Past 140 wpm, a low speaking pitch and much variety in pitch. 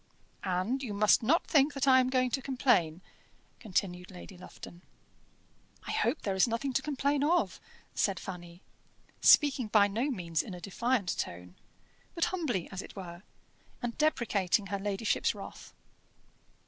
No: average, 150 wpm; high, 210 Hz; wide, 6.4 semitones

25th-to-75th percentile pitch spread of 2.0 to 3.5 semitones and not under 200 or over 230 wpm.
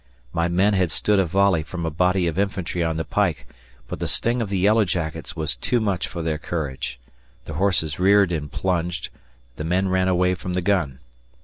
Yes: average, 3.1 semitones; fast, 205 wpm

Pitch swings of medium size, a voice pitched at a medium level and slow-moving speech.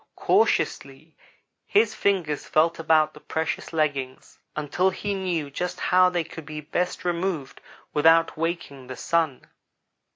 Yes: average, 3.2 semitones; medium, 165 Hz; slow, 130 wpm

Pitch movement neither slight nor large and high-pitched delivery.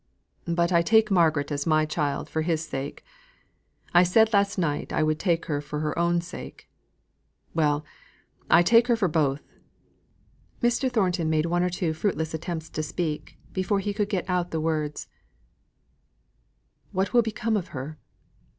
No: average, 3.8 semitones; medium, 170 Hz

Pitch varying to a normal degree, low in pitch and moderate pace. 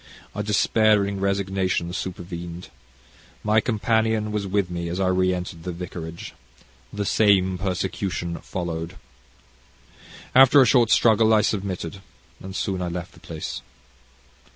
No: average, 3.1 semitones; very low, 95 Hz; slow, 130 wpm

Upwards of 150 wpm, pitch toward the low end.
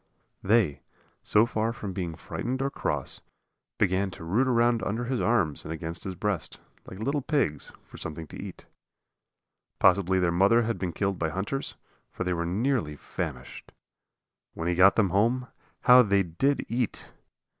Yes: average, 165 wpm; low, 100 Hz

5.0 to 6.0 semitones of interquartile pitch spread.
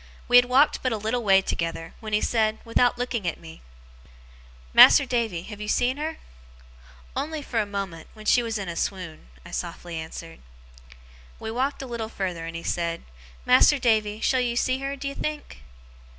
Yes: wide, 5.4 semitones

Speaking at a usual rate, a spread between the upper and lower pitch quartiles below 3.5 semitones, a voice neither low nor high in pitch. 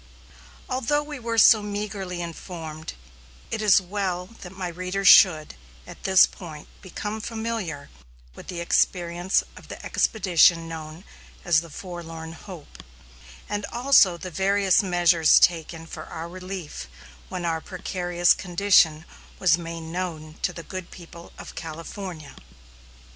No: slow, 130 wpm; average, 2.8 semitones; medium, 180 Hz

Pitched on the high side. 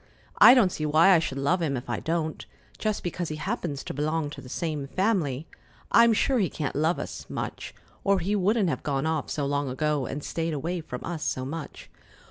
No: medium, 160 Hz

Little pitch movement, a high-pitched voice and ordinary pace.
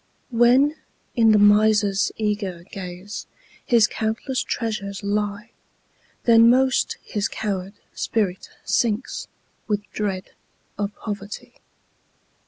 No: narrow, 2.2 semitones; high, 210 Hz; slow, 90 wpm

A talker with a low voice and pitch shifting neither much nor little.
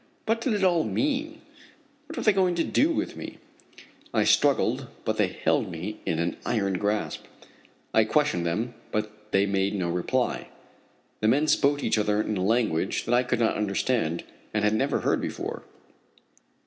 No: low, 110 Hz; wide, 7.1 semitones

